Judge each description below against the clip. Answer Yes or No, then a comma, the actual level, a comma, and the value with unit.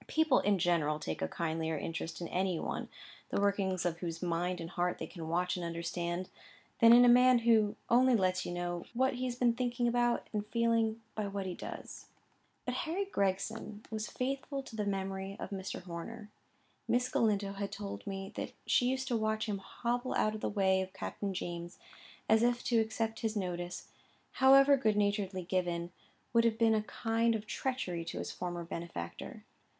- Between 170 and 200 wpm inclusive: Yes, average, 190 wpm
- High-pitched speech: Yes, high, 205 Hz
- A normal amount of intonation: Yes, average, 4.7 semitones